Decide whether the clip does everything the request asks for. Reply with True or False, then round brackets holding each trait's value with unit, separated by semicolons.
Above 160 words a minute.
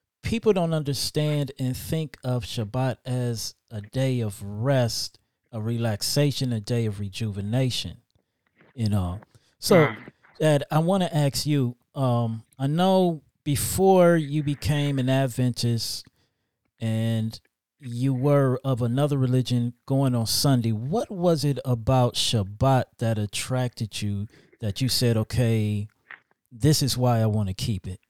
False (135 wpm)